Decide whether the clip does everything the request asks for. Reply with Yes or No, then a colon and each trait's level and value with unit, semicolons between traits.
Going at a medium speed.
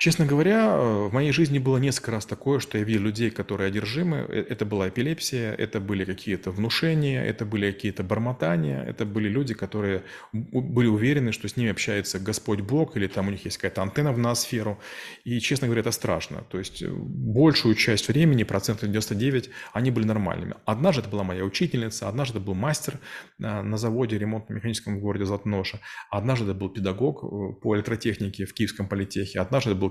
No: fast, 175 wpm